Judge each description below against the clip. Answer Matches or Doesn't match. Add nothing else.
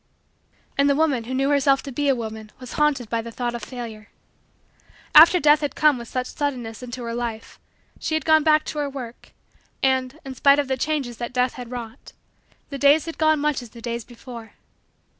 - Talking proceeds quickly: Matches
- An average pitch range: Matches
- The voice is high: Matches